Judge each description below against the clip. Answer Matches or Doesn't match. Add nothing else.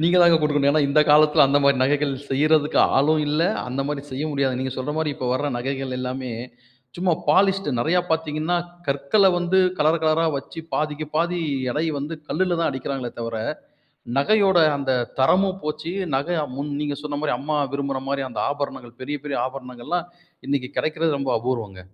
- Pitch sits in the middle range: Matches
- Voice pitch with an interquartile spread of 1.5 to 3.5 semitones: Matches